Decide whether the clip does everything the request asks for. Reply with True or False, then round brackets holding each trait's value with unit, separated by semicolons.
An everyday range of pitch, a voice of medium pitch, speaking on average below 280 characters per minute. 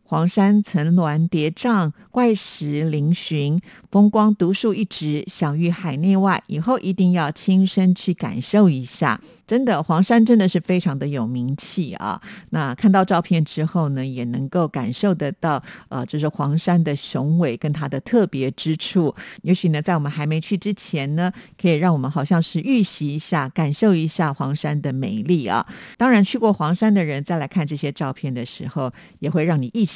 True (4.5 semitones; 170 Hz; 270 characters per minute)